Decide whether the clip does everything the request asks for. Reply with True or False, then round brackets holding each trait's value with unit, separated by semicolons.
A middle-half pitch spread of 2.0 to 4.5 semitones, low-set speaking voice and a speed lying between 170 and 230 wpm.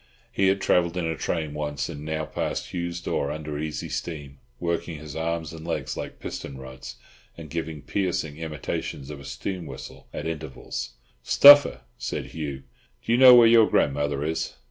True (2.8 semitones; 80 Hz; 175 wpm)